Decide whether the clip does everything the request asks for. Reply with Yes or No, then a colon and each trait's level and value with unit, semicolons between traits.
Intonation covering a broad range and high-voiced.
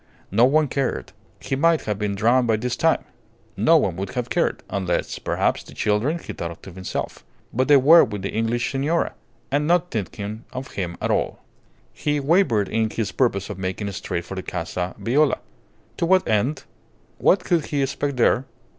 No: wide, 6.4 semitones; low, 120 Hz